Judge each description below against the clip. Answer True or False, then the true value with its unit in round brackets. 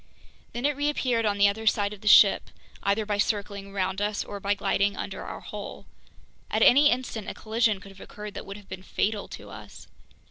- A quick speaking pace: True (210 wpm)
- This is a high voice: True (205 Hz)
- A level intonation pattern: True (1.8 semitones)